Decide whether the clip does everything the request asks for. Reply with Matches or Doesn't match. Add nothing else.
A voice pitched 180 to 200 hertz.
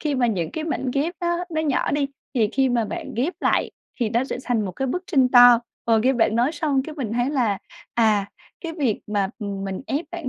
Doesn't match